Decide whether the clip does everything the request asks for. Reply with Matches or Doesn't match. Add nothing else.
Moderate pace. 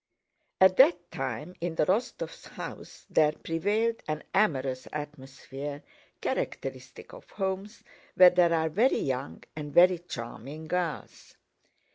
Doesn't match